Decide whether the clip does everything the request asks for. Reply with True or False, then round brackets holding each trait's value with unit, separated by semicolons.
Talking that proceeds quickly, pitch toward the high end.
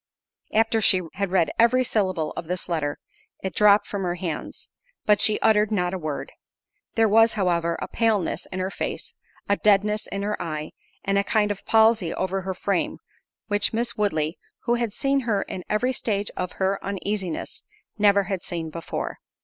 False (180 wpm; 200 Hz)